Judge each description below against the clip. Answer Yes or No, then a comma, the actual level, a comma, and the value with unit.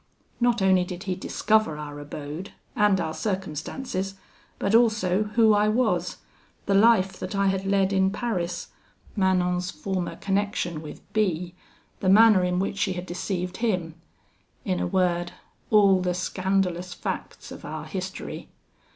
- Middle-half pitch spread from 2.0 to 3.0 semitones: Yes, narrow, 2.4 semitones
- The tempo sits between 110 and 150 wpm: Yes, average, 145 wpm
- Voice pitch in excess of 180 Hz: Yes, high, 190 Hz